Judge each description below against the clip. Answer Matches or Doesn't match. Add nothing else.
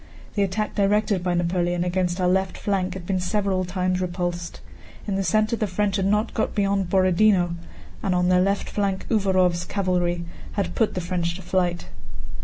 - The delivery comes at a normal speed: Matches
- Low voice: Doesn't match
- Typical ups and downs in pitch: Doesn't match